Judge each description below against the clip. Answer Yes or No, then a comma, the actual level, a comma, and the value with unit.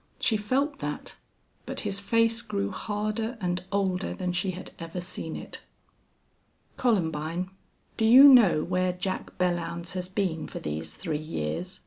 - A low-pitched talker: No, medium, 185 Hz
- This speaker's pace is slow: No, average, 145 wpm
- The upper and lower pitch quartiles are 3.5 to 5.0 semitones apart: Yes, average, 4.0 semitones